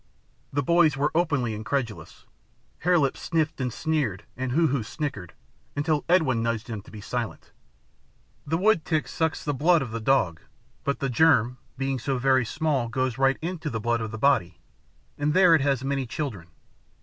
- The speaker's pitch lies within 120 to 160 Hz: Yes, low, 135 Hz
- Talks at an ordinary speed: Yes, average, 175 wpm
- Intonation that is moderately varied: Yes, average, 4.9 semitones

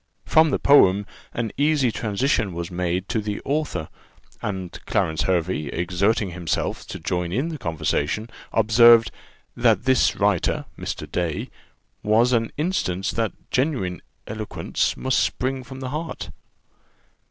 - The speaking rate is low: Yes, slow, 130 wpm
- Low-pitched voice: Yes, low, 110 Hz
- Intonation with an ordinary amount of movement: No, wide, 6.3 semitones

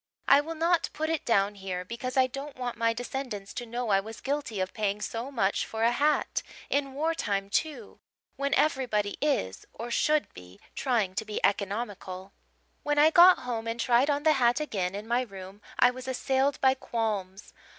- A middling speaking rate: Yes, average, 190 wpm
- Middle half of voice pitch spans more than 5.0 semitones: Yes, wide, 5.4 semitones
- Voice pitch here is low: No, high, 240 Hz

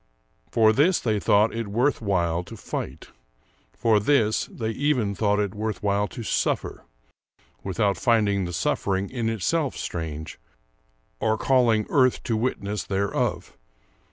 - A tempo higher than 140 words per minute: No, slow, 135 wpm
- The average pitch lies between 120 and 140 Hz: No, low, 110 Hz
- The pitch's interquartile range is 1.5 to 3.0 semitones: Yes, average, 2.7 semitones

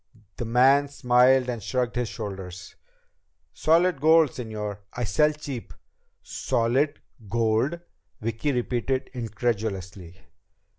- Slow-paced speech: Yes, slow, 100 wpm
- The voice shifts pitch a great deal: No, average, 3.8 semitones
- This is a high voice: No, low, 120 Hz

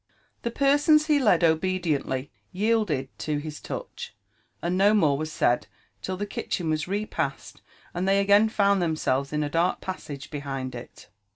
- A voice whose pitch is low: No, medium, 175 Hz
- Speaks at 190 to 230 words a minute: No, average, 160 wpm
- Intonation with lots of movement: Yes, wide, 5.7 semitones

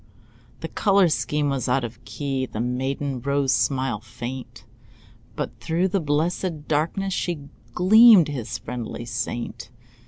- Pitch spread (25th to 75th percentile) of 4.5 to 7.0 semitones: Yes, average, 5.1 semitones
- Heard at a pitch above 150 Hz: No, medium, 140 Hz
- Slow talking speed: Yes, slow, 130 wpm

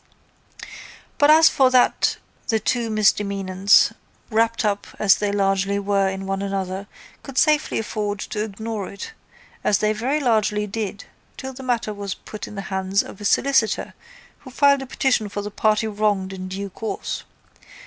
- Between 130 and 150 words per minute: No, average, 165 wpm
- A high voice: Yes, high, 210 Hz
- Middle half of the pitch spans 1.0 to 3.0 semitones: Yes, average, 2.7 semitones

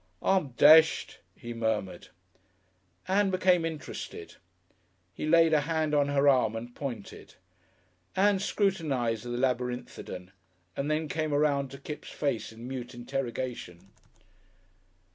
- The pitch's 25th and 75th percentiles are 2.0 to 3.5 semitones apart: No, average, 4.7 semitones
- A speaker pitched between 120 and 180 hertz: Yes, medium, 140 Hz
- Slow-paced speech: Yes, slow, 120 wpm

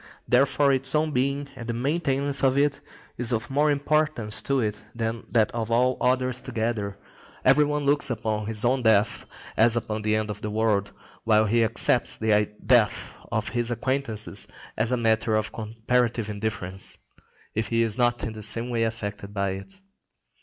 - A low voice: Yes, low, 115 Hz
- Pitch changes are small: No, average, 3.2 semitones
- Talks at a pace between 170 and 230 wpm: Yes, average, 175 wpm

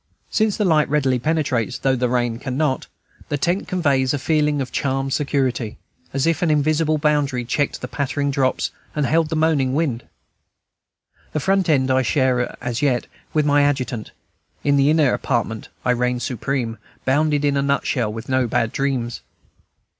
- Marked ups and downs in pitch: No, average, 3.1 semitones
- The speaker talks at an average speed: Yes, average, 170 wpm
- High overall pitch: No, medium, 140 Hz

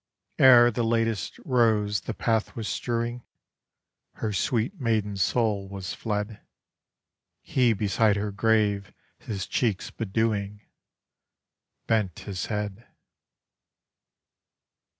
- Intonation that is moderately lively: No, narrow, 2.3 semitones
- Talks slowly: Yes, slow, 95 wpm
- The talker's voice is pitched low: Yes, low, 110 Hz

